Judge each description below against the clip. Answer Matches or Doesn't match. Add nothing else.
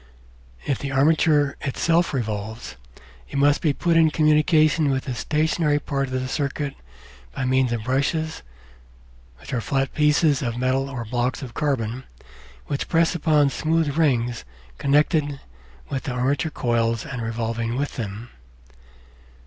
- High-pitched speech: Doesn't match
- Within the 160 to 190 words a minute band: Doesn't match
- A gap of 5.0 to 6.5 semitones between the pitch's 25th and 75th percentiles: Doesn't match